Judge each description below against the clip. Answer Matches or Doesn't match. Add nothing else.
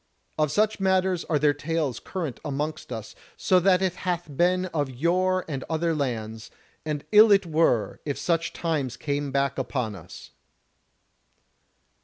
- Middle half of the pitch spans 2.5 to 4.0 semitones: Doesn't match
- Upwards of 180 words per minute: Doesn't match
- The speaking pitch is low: Doesn't match